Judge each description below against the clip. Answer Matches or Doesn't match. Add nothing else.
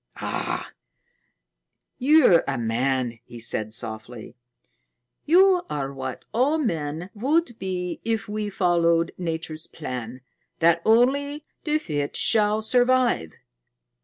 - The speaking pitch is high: Doesn't match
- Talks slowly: Matches